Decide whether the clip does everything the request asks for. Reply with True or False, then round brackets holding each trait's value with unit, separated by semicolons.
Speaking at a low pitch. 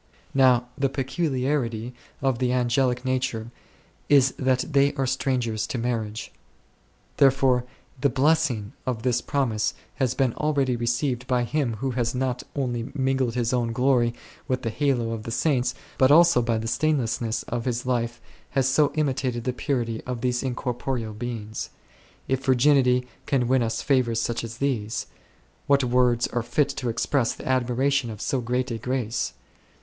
True (125 Hz)